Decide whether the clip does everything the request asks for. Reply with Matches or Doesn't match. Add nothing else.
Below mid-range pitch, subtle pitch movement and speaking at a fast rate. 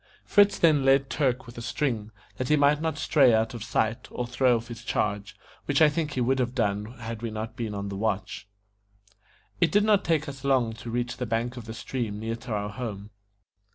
Doesn't match